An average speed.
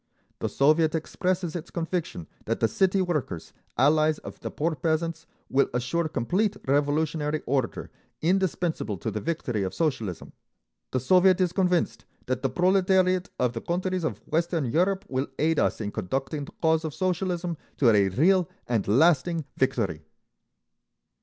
Yes: average, 150 wpm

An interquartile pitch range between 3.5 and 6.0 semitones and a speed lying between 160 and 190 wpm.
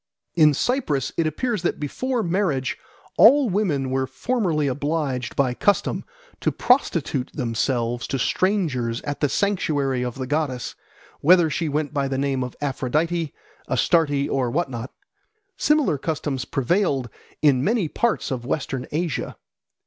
No: average, 4.9 semitones; average, 140 wpm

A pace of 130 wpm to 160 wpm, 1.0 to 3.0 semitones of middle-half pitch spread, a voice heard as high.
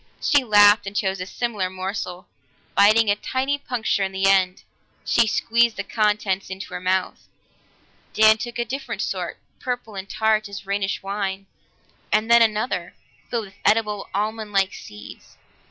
Yes: average, 155 wpm; average, 2.7 semitones; high, 205 Hz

